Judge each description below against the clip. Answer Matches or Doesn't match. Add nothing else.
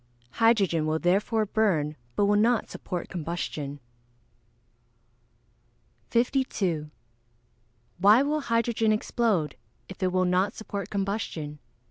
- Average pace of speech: Doesn't match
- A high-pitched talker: Matches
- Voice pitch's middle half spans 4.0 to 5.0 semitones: Matches